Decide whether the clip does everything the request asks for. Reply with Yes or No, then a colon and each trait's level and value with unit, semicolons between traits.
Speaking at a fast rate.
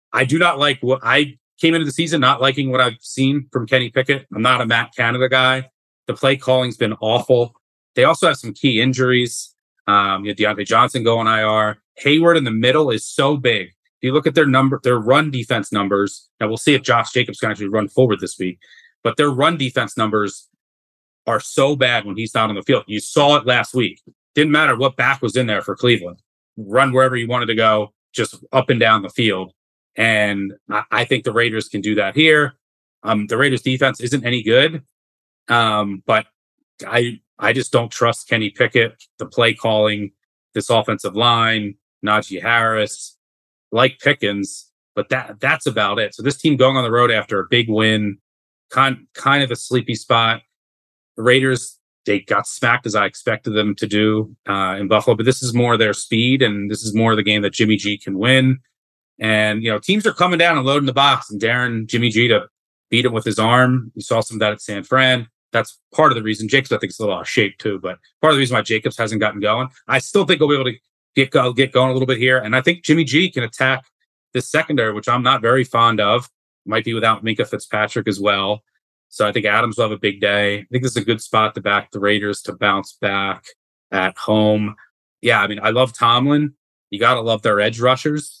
Yes: fast, 220 wpm